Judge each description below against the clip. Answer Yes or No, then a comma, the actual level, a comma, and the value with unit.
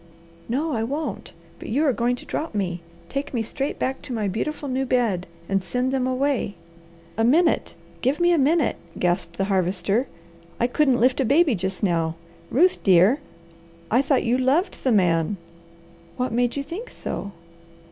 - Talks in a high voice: Yes, very high, 250 Hz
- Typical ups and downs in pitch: No, wide, 5.8 semitones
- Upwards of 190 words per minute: No, average, 175 wpm